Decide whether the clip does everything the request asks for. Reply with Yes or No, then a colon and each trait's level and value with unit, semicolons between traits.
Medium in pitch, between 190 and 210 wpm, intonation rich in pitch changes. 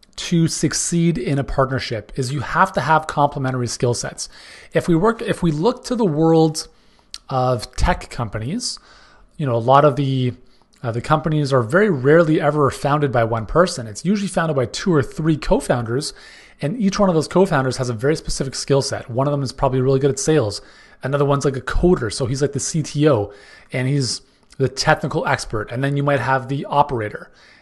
No: medium, 145 Hz; average, 200 wpm; average, 3.9 semitones